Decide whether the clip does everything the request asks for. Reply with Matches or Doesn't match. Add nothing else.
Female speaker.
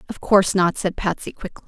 Matches